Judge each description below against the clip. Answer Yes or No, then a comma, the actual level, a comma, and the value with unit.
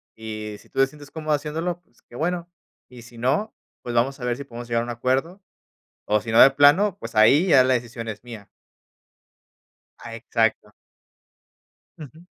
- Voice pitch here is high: No, low, 125 Hz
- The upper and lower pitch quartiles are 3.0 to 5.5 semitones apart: Yes, average, 4.6 semitones